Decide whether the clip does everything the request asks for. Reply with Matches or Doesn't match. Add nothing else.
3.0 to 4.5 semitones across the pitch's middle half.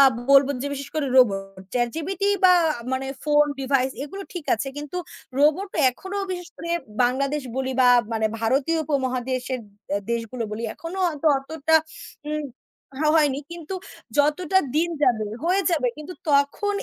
Matches